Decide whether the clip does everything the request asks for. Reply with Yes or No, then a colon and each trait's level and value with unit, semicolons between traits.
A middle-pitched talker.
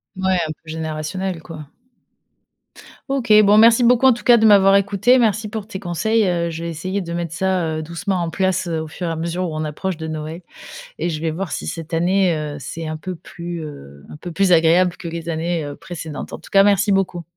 Yes: medium, 175 Hz